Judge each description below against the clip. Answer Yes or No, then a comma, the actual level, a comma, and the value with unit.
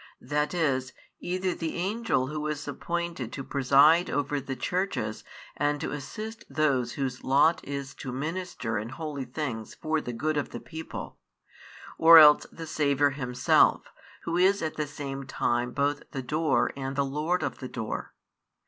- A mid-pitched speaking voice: Yes, medium, 145 Hz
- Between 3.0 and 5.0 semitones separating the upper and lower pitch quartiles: Yes, average, 3.3 semitones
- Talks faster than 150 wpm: Yes, average, 165 wpm